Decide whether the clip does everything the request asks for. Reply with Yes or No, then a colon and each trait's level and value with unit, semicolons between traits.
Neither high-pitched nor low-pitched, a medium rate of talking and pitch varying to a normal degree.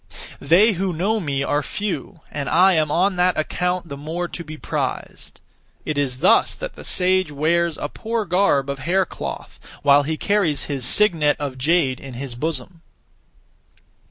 Yes: medium, 160 Hz; average, 170 wpm; average, 4.3 semitones